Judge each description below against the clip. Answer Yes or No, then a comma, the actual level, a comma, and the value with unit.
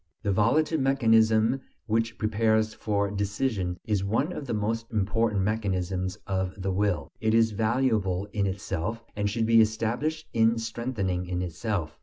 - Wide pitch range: No, average, 2.8 semitones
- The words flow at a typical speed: Yes, average, 150 wpm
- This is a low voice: Yes, low, 110 Hz